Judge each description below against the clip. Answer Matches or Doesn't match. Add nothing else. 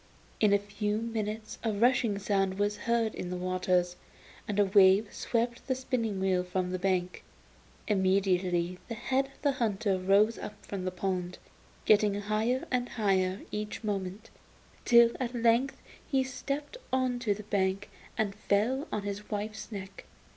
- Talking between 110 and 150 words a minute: Doesn't match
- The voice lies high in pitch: Matches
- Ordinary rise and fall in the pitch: Matches